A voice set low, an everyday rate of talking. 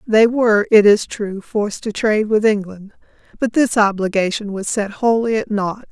No: high, 210 Hz; average, 185 wpm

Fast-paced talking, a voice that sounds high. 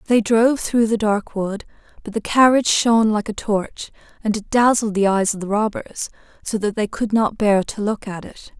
Yes: fast, 215 wpm; high, 215 Hz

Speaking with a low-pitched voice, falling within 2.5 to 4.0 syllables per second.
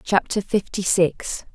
No: medium, 185 Hz; 3.6 syllables/s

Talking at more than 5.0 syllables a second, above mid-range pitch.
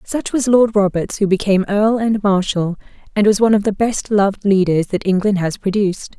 Yes: 5.5 syllables/s; high, 200 Hz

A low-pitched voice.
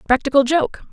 No: very high, 280 Hz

